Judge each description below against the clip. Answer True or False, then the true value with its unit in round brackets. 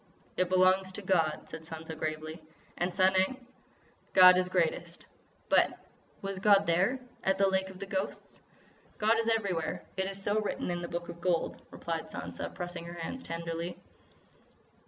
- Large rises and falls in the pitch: False (2.4 semitones)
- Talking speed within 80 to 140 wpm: False (150 wpm)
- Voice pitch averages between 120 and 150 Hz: False (185 Hz)